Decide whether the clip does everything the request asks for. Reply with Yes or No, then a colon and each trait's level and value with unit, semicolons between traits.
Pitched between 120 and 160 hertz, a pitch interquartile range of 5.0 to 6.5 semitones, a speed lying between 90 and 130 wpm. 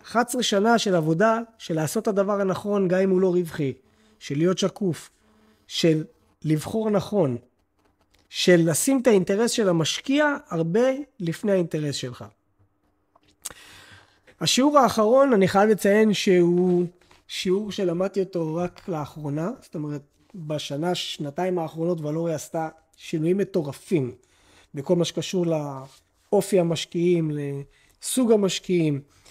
No: medium, 175 Hz; wide, 5.4 semitones; average, 115 wpm